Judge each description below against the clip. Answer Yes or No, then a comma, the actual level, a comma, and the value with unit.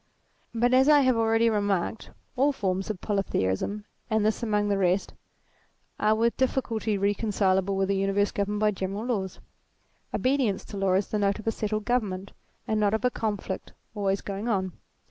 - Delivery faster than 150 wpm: Yes, average, 180 wpm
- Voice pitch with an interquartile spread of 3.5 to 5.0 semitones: No, narrow, 2.5 semitones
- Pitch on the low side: No, high, 210 Hz